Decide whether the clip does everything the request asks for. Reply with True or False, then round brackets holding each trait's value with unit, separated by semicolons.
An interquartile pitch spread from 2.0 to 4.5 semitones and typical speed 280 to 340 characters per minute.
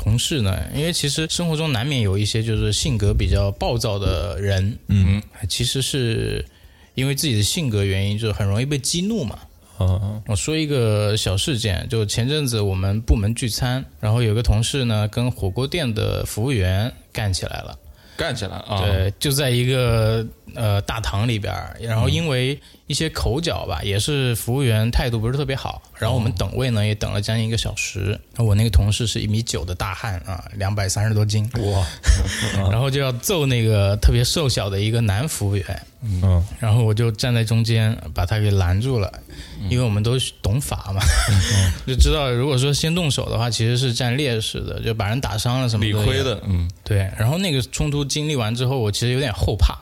True (3.8 semitones; 295 characters per minute)